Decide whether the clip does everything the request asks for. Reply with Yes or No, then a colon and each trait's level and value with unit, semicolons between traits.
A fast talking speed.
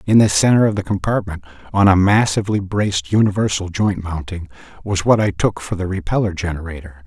No: average, 180 wpm